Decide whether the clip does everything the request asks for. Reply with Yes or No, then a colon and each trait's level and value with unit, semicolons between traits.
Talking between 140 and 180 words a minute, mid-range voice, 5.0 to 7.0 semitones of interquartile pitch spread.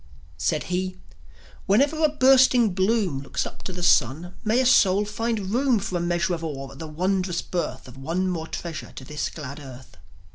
No: average, 190 wpm; medium, 180 Hz; wide, 5.5 semitones